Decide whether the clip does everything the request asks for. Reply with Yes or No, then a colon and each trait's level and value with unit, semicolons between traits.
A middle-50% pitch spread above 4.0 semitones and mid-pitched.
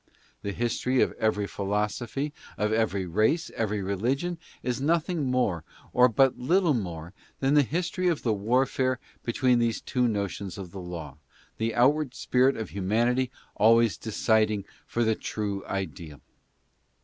No: average, 4.5 semitones; low, 115 Hz